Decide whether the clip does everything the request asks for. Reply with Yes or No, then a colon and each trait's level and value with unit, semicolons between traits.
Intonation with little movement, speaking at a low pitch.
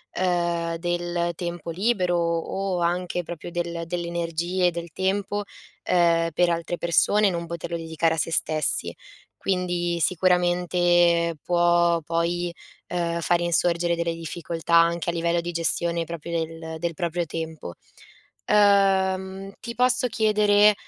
No: narrow, 1.2 semitones; medium, 175 Hz